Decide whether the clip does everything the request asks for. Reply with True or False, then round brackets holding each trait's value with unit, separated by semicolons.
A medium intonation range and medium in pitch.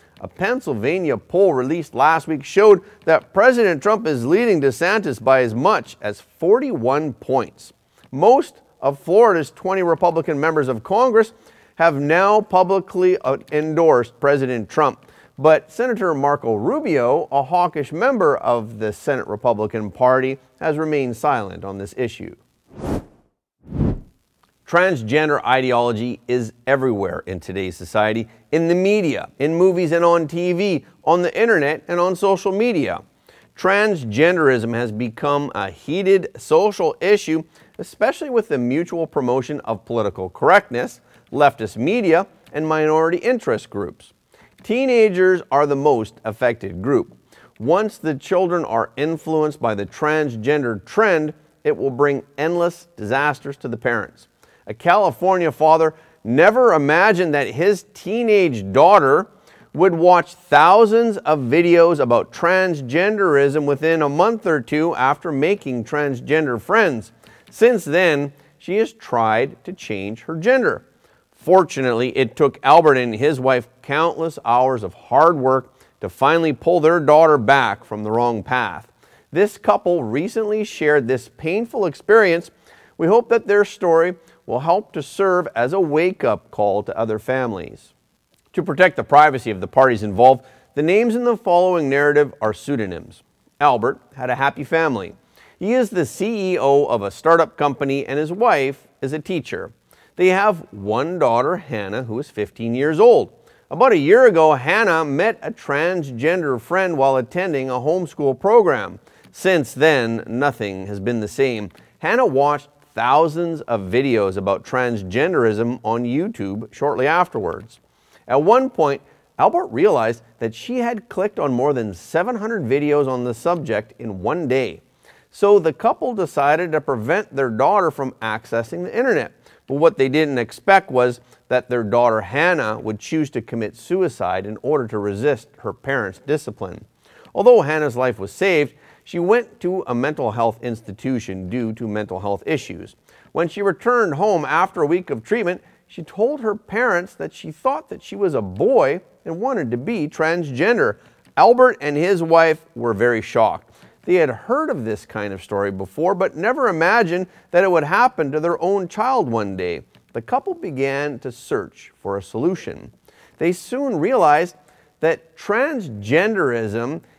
False (6.6 semitones; 150 Hz)